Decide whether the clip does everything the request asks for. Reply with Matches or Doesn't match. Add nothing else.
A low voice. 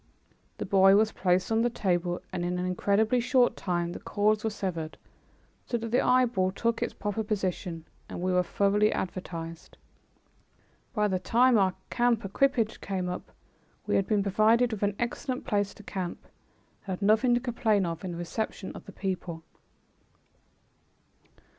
Doesn't match